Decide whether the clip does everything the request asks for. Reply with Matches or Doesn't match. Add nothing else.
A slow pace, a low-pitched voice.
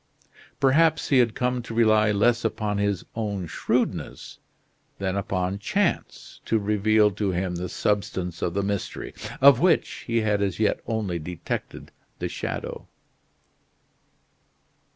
Matches